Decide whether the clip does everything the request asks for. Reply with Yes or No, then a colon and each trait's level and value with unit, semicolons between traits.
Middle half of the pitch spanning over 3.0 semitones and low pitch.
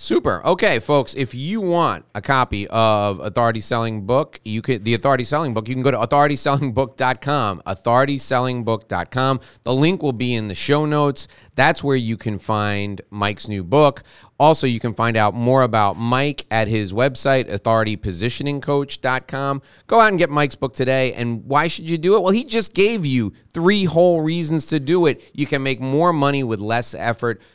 Yes: average, 4.1 semitones; low, 130 Hz